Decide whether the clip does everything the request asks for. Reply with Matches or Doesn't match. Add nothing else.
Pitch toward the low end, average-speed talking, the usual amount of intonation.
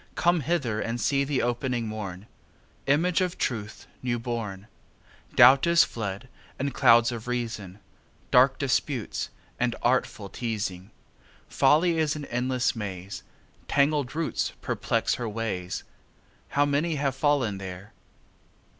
Doesn't match